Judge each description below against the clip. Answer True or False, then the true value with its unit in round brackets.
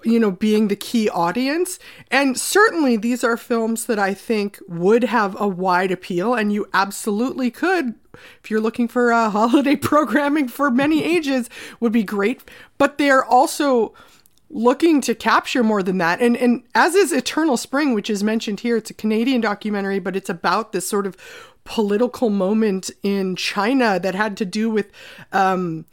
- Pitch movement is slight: False (4.2 semitones)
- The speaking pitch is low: False (230 Hz)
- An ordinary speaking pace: True (175 wpm)